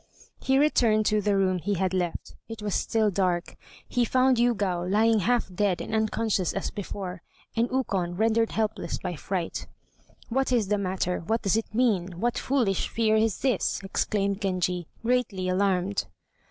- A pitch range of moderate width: Yes, average, 3.5 semitones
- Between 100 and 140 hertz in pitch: No, high, 205 Hz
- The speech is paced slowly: No, average, 165 wpm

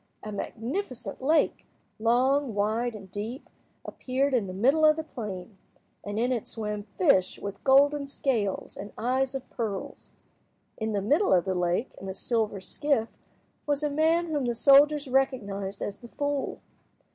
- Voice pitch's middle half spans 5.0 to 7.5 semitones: Yes, wide, 5.4 semitones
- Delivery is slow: No, average, 155 wpm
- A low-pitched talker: No, high, 240 Hz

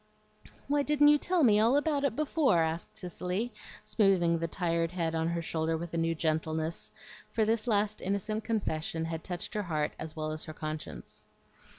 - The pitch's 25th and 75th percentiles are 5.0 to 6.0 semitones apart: Yes, average, 5.3 semitones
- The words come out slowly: No, average, 185 wpm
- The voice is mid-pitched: Yes, medium, 175 Hz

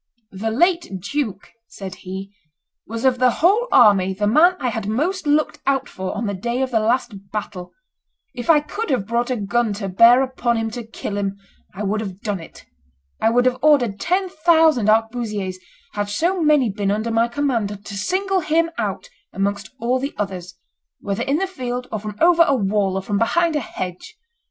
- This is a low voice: No, high, 230 Hz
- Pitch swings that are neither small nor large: No, wide, 5.9 semitones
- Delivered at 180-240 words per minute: Yes, average, 195 wpm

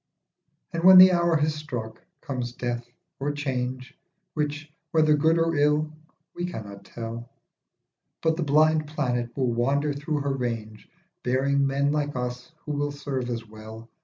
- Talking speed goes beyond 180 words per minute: No, average, 155 wpm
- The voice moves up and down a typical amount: Yes, average, 3.8 semitones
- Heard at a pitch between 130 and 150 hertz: Yes, medium, 140 Hz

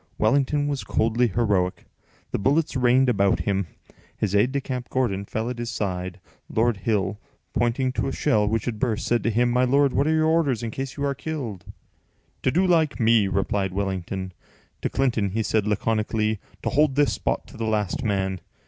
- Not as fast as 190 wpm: No, average, 195 wpm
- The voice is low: Yes, low, 115 Hz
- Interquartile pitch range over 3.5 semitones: Yes, average, 4.7 semitones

